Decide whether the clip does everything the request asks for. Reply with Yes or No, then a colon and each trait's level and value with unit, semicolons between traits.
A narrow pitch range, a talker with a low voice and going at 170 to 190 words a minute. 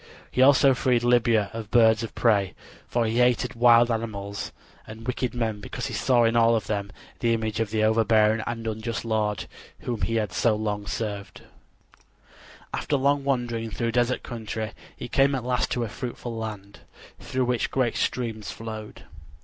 Yes: narrow, 2.0 semitones; low, 115 Hz; average, 175 wpm